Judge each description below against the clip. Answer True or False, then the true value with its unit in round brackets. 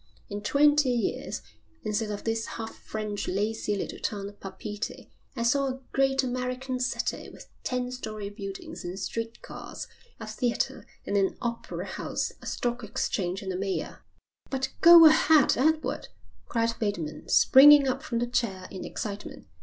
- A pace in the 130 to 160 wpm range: True (155 wpm)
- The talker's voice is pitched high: True (230 Hz)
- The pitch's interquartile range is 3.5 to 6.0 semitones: True (3.9 semitones)